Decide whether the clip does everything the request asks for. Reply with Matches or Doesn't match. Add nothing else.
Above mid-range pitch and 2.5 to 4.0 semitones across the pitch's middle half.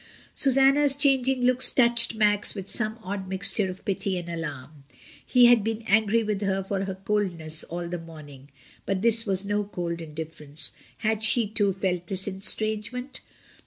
Doesn't match